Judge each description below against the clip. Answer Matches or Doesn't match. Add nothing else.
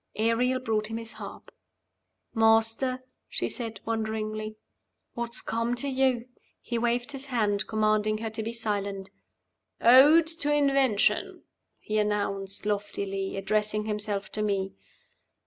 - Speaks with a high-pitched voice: Matches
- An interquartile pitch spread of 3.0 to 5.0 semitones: Doesn't match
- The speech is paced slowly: Matches